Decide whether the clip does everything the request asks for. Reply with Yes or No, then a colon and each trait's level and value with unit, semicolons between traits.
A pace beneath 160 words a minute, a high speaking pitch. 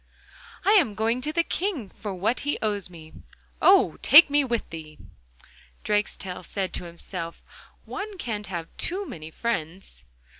Yes: average, 150 wpm; high, 210 Hz